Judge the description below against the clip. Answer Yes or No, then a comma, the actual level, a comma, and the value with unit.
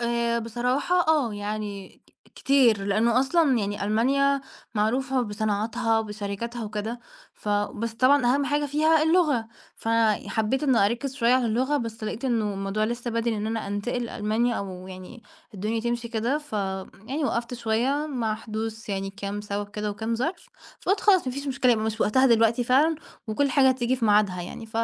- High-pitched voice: Yes, high, 230 Hz